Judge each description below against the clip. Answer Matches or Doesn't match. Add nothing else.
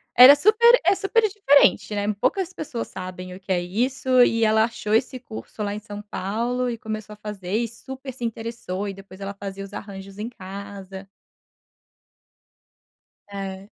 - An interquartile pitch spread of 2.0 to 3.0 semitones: Doesn't match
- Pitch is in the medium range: Doesn't match